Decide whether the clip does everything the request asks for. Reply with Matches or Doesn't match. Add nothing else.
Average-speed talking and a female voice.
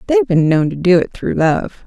Doesn't match